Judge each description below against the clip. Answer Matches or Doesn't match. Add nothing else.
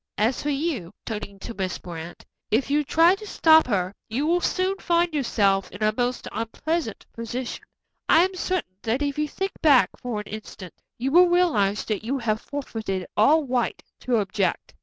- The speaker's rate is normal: Matches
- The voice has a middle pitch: Doesn't match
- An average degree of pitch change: Doesn't match